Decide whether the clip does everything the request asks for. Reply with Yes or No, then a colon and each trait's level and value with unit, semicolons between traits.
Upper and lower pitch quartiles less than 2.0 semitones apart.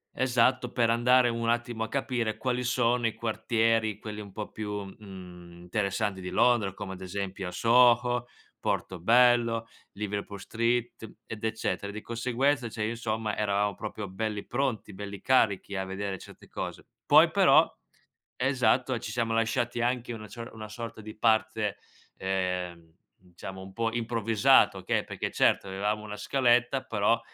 No: average, 2.9 semitones